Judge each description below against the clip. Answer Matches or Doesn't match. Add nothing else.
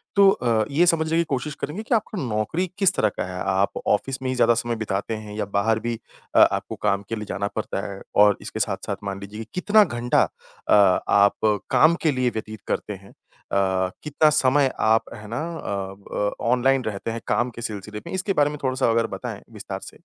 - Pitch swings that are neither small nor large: Doesn't match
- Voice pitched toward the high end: Doesn't match